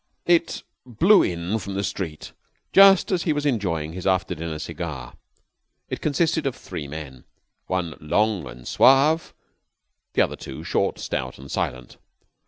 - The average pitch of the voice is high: No, very low, 95 Hz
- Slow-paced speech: No, average, 150 wpm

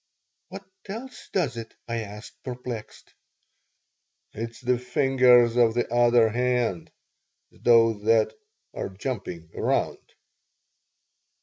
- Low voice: Yes, low, 120 Hz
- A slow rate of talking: Yes, slow, 100 wpm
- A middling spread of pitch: No, narrow, 2.0 semitones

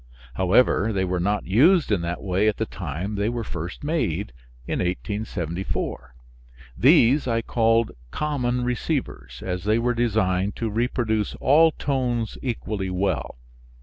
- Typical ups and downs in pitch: Yes, average, 4.7 semitones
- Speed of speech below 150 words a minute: Yes, average, 140 wpm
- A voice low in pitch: Yes, low, 110 Hz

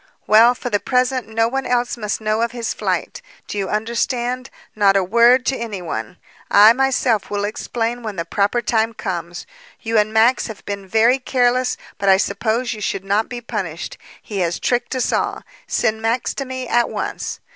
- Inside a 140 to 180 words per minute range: No, average, 190 wpm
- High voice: Yes, high, 225 Hz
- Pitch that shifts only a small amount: No, average, 3.2 semitones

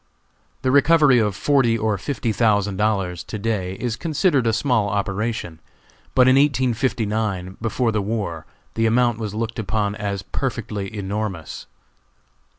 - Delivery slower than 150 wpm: Yes, average, 140 wpm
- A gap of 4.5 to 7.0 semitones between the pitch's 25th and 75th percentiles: No, average, 3.3 semitones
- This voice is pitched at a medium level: No, low, 110 Hz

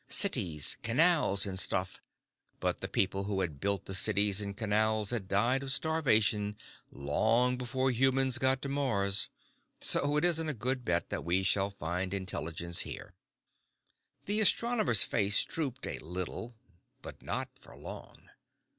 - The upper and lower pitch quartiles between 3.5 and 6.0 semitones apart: Yes, wide, 5.5 semitones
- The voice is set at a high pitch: No, low, 110 Hz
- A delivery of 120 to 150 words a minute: Yes, average, 145 wpm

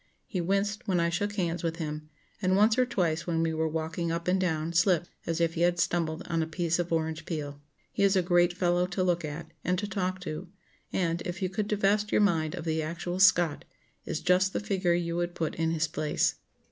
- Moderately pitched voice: Yes, medium, 175 Hz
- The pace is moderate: No, fast, 230 wpm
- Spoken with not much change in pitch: Yes, narrow, 2.3 semitones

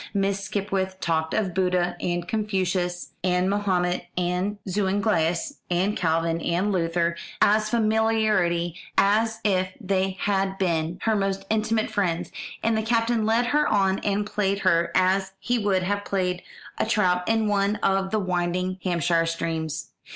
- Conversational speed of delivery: Yes, average, 145 wpm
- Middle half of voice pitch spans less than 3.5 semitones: Yes, average, 2.9 semitones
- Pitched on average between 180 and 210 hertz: Yes, high, 190 Hz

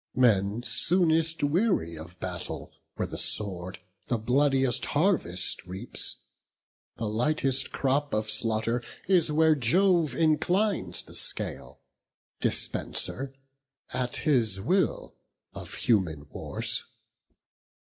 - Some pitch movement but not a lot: No, wide, 7.4 semitones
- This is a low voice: Yes, low, 130 Hz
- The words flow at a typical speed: No, slow, 100 wpm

